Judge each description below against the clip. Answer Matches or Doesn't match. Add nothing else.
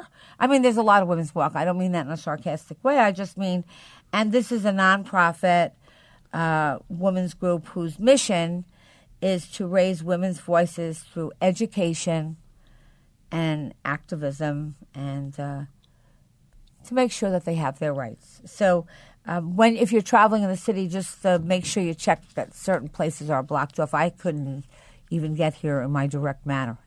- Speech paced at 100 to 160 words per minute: Doesn't match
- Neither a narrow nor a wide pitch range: Matches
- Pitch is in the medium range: Matches